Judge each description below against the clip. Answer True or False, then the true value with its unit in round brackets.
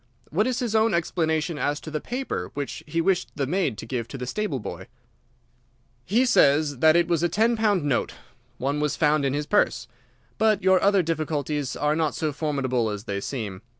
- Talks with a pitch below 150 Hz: False (155 Hz)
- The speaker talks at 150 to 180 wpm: False (200 wpm)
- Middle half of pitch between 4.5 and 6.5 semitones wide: True (5.3 semitones)